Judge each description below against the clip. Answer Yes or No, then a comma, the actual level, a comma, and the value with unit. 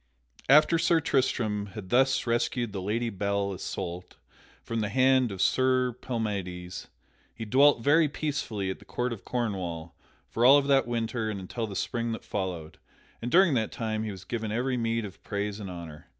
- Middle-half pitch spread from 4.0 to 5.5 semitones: Yes, average, 4.4 semitones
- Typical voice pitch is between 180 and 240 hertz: No, low, 115 Hz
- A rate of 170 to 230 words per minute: Yes, average, 185 wpm